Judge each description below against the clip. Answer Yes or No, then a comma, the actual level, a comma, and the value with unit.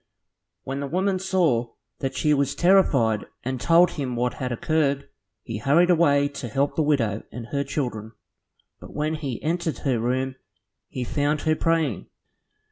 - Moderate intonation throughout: Yes, average, 4.2 semitones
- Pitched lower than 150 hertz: Yes, medium, 140 Hz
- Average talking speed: Yes, average, 160 wpm